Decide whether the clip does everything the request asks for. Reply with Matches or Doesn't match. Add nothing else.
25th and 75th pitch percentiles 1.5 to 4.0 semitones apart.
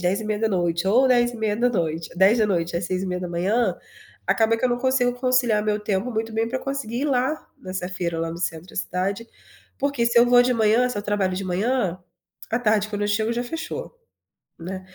Doesn't match